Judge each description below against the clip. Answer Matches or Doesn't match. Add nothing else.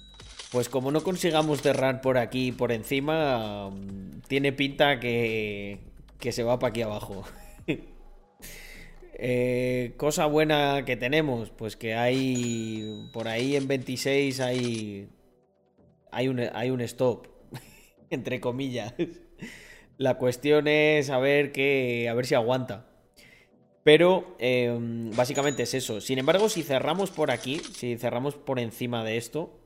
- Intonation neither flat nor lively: Matches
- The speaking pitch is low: Matches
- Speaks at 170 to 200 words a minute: Doesn't match